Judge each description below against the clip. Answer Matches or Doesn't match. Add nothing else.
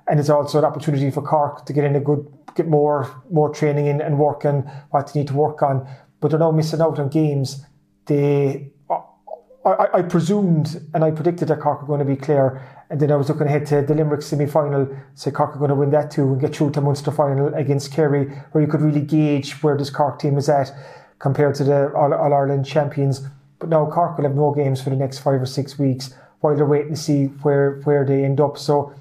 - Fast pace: Matches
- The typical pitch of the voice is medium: Matches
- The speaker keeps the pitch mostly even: Matches